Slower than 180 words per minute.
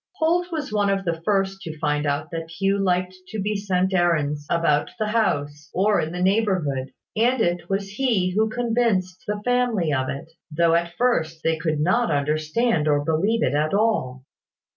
No: average, 185 wpm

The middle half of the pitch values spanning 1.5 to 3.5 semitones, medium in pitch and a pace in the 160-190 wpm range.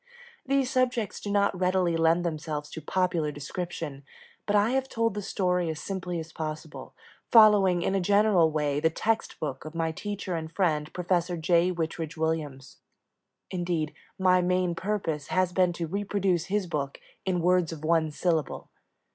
Yes: average, 3.1 semitones; medium, 175 Hz; average, 165 wpm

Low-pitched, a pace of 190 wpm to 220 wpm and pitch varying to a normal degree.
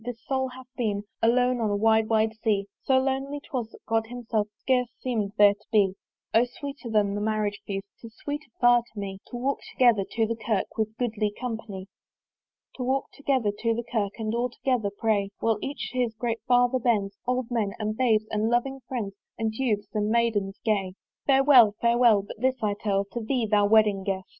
No: high, 225 Hz; average, 200 wpm; average, 3.0 semitones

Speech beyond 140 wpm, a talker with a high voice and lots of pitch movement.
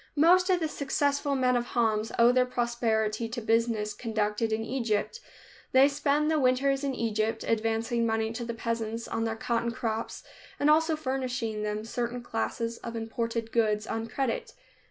No: average, 165 wpm; high, 230 Hz; average, 2.7 semitones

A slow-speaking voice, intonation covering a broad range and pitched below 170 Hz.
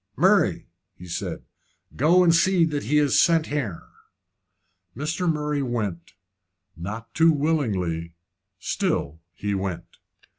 Yes: slow, 115 wpm; wide, 9.0 semitones; low, 135 Hz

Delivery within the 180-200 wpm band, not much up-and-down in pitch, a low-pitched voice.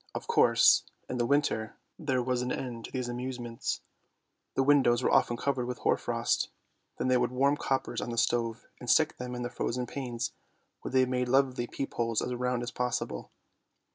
Yes: average, 195 wpm; narrow, 1.4 semitones; low, 125 Hz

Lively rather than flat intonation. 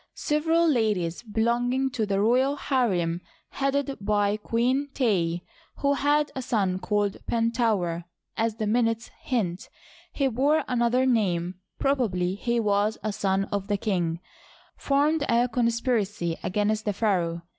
No: average, 4.5 semitones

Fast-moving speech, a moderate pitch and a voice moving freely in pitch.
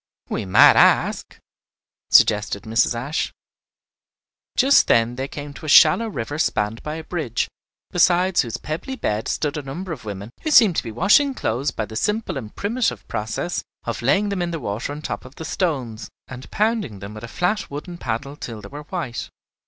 No: average, 190 wpm; medium, 145 Hz; wide, 7.6 semitones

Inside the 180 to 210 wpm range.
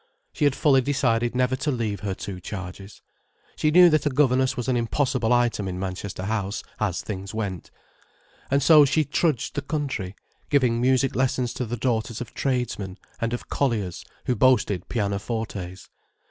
No: average, 165 wpm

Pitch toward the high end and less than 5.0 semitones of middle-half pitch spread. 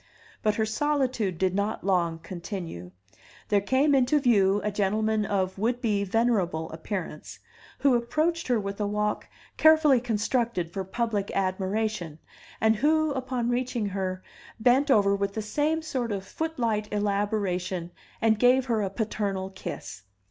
Yes: high, 210 Hz; average, 4.2 semitones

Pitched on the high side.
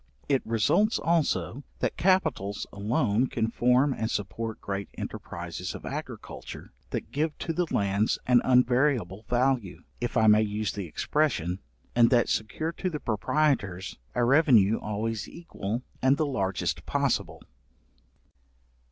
No: low, 120 Hz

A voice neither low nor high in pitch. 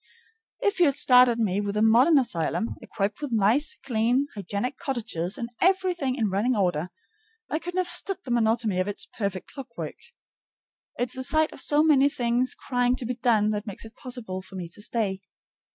No: high, 235 Hz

